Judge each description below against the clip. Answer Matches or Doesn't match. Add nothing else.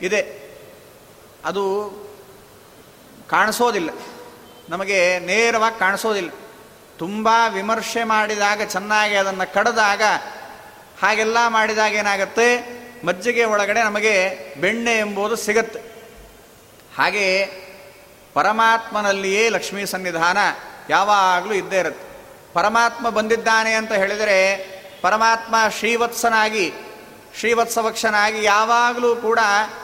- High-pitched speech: Matches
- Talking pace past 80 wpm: Doesn't match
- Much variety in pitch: Doesn't match